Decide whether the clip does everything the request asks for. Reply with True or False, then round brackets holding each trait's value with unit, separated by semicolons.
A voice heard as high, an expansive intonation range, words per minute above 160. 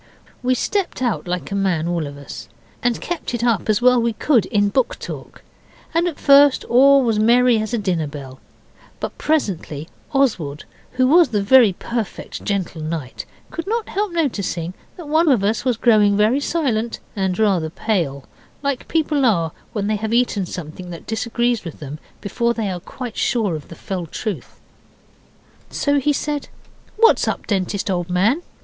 True (220 Hz; 6.3 semitones; 180 wpm)